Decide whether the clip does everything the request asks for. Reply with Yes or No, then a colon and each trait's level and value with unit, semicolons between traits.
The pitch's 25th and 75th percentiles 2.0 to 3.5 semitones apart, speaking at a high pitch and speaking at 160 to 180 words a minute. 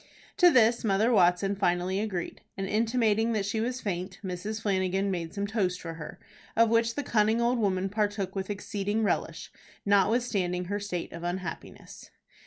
Yes: average, 3.1 semitones; high, 200 Hz; average, 165 wpm